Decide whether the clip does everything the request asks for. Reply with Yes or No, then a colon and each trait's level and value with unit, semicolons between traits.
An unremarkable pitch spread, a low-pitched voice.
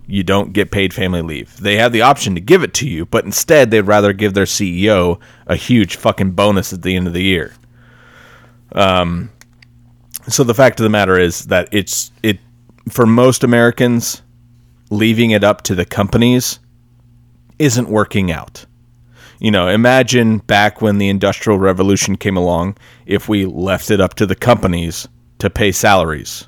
Yes: average, 3.9 semitones; low, 105 Hz